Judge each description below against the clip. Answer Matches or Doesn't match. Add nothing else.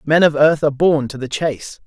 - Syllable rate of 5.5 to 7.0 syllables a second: Matches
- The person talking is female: Doesn't match